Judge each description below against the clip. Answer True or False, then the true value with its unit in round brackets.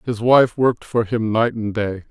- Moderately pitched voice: False (115 Hz)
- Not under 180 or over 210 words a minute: False (230 wpm)